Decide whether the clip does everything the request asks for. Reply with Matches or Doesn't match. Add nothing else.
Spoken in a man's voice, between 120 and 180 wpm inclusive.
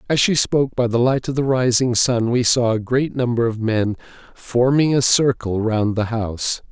Doesn't match